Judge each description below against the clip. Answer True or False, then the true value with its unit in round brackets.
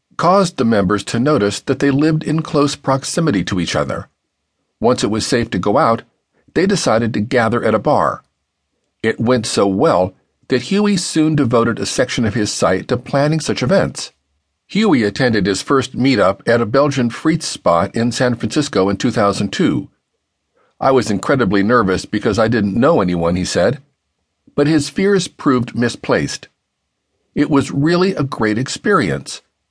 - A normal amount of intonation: False (6.0 semitones)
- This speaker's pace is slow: False (165 wpm)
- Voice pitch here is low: True (120 Hz)